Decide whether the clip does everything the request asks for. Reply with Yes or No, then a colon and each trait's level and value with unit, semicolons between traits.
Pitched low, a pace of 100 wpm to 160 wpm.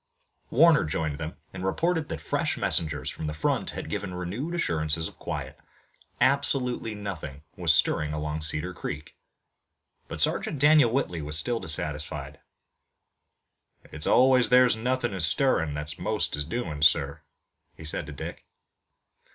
Yes: very low, 80 Hz; average, 145 wpm